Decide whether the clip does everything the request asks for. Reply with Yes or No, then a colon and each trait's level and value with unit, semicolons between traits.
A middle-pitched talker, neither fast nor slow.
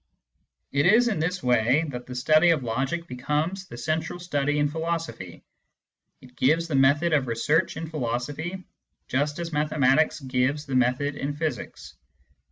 Yes: medium, 145 Hz; average, 155 wpm